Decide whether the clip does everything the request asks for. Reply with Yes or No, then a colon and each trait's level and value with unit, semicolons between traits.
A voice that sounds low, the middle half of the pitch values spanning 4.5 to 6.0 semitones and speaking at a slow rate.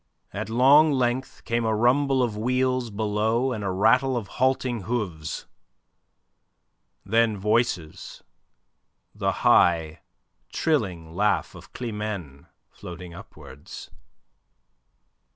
Yes: low, 110 Hz; average, 4.8 semitones; slow, 100 wpm